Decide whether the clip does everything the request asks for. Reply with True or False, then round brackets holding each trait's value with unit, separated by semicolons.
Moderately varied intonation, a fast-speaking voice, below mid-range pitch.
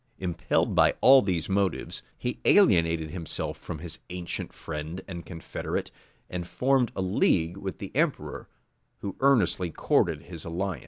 False (3.2 semitones; 145 wpm; 90 Hz)